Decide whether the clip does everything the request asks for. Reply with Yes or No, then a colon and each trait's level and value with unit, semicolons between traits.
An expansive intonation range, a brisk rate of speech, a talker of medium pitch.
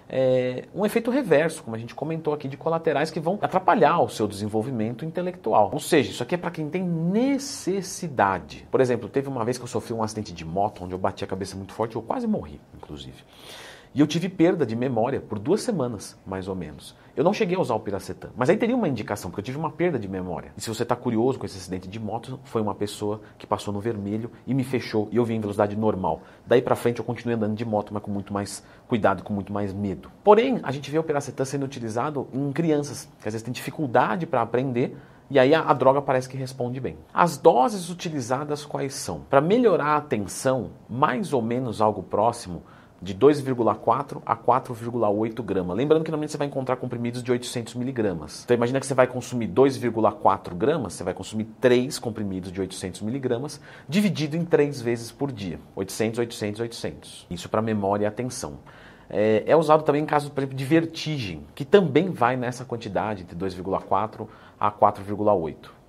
No: wide, 5.7 semitones; fast, 205 wpm; low, 120 Hz